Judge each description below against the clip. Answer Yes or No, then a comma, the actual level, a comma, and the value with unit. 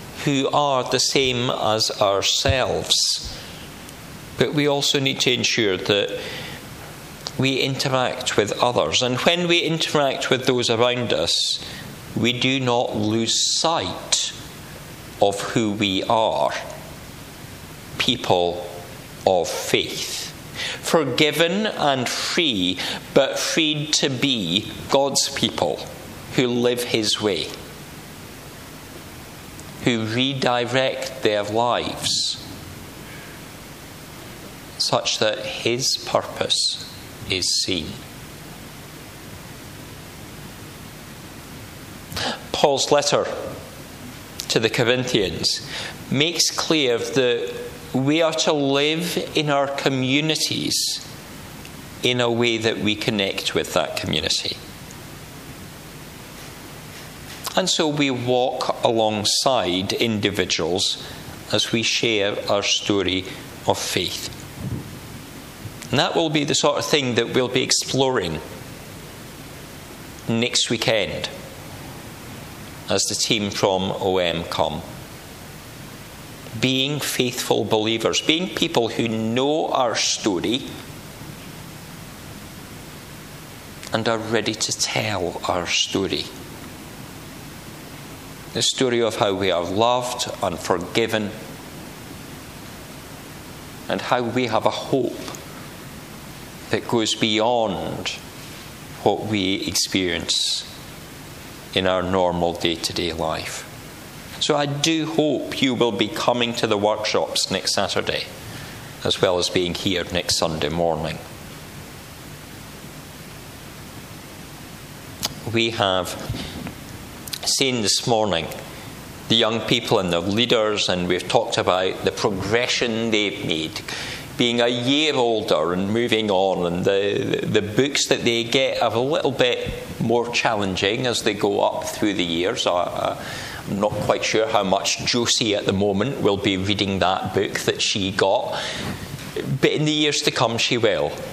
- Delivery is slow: Yes, slow, 110 wpm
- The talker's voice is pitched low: Yes, low, 120 Hz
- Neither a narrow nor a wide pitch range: Yes, average, 4.5 semitones